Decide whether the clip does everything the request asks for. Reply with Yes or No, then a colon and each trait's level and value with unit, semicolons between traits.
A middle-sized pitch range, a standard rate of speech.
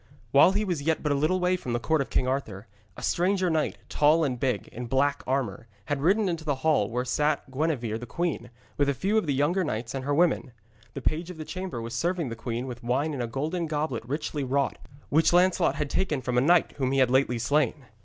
No: average, 4.5 semitones; fast, 240 wpm